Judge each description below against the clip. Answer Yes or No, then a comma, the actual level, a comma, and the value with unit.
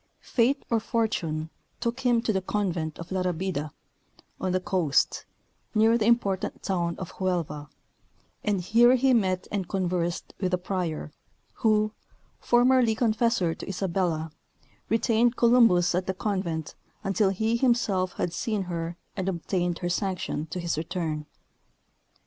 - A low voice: No, high, 190 Hz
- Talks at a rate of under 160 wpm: Yes, average, 140 wpm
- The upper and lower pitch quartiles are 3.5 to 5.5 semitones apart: Yes, average, 4.4 semitones